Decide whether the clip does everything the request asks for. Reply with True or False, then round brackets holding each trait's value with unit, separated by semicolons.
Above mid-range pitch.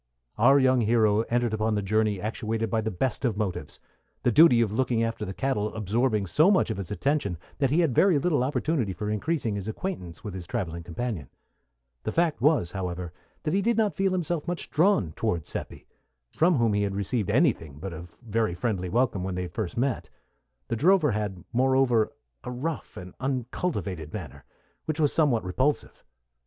False (115 Hz)